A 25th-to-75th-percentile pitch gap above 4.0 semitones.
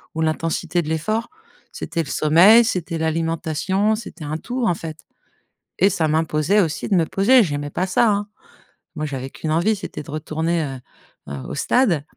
Yes: average, 4.4 semitones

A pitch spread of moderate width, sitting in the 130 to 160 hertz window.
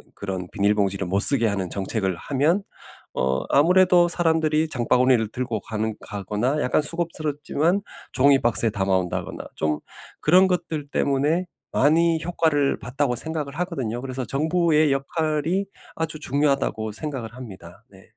No: wide, 6.6 semitones; medium, 140 Hz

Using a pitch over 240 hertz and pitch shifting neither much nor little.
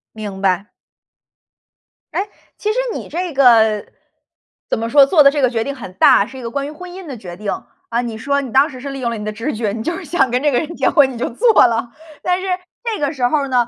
Yes: very high, 260 Hz; average, 4.6 semitones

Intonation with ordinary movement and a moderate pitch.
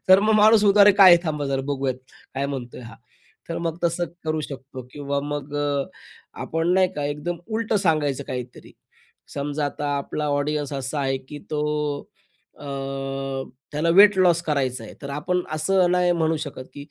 Yes: average, 3.9 semitones; medium, 150 Hz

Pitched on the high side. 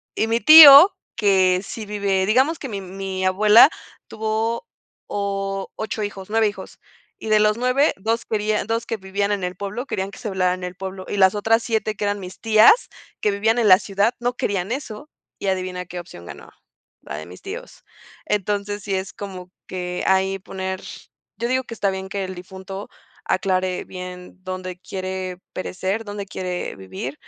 Yes: high, 195 Hz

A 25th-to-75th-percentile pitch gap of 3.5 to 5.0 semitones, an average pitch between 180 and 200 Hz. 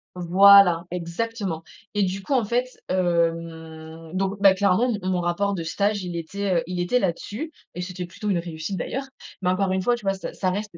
No: average, 2.9 semitones; medium, 185 Hz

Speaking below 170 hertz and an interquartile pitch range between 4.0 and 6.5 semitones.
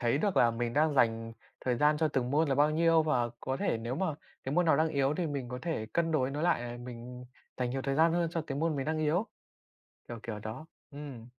Yes: medium, 140 Hz; average, 4.5 semitones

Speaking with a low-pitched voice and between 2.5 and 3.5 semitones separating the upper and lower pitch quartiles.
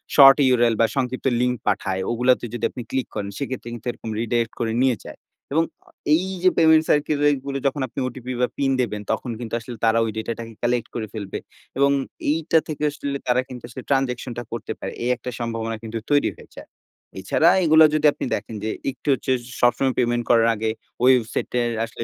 Yes: low, 125 Hz; average, 3.2 semitones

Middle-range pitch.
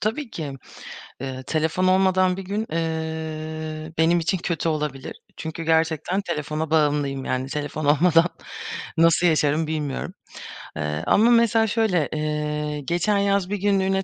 Yes: medium, 160 Hz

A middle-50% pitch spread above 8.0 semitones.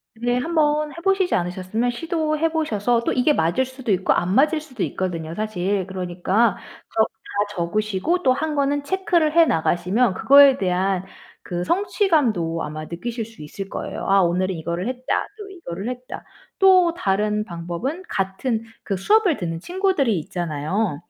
Yes: wide, 8.6 semitones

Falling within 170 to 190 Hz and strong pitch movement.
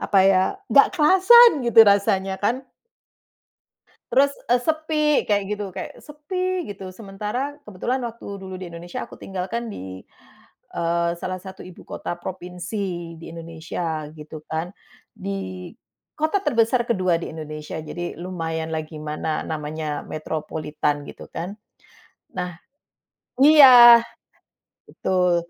Yes: medium, 185 Hz; wide, 6.1 semitones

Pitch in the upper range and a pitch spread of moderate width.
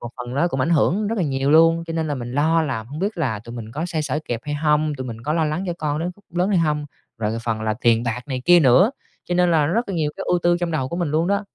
No: medium, 150 Hz; average, 5.0 semitones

